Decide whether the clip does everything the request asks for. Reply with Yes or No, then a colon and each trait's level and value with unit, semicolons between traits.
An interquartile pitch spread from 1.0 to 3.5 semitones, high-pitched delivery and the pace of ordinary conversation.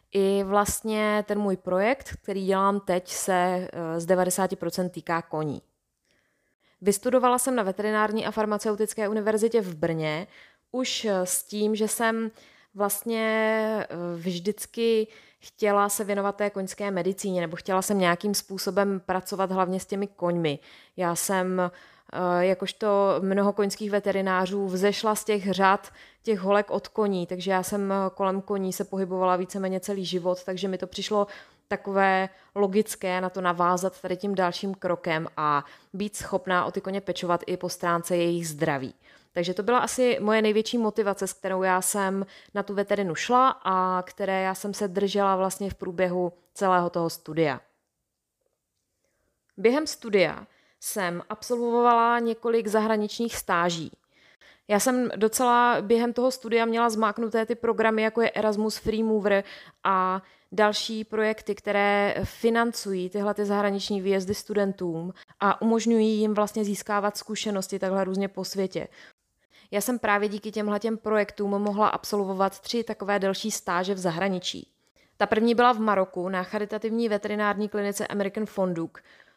Yes: narrow, 2.5 semitones; high, 200 Hz; average, 145 wpm